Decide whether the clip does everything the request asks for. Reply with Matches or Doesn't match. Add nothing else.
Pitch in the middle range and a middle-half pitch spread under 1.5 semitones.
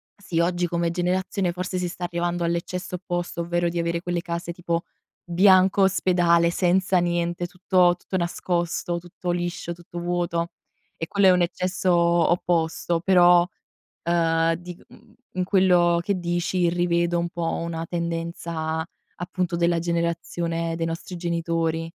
Matches